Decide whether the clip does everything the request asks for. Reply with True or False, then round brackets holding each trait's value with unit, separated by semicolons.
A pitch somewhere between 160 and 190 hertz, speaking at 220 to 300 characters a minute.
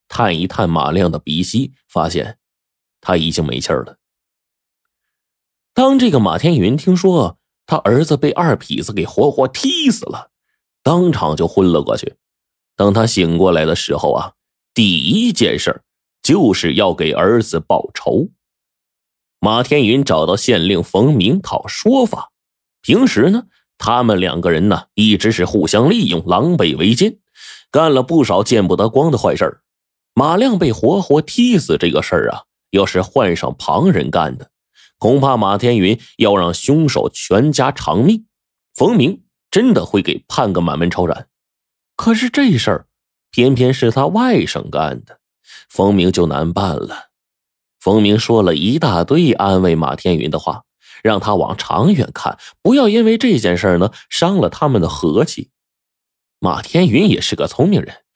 False (120 Hz; 225 characters per minute)